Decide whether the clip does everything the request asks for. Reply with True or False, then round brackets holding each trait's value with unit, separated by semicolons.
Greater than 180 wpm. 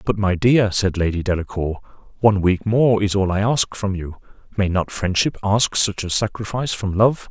True (190 wpm)